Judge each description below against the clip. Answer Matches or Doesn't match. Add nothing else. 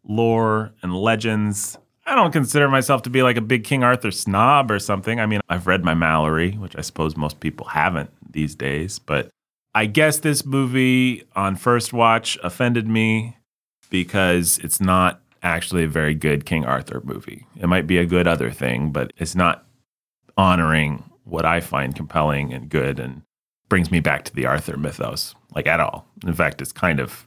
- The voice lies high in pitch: Doesn't match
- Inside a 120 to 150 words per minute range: Doesn't match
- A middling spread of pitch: Doesn't match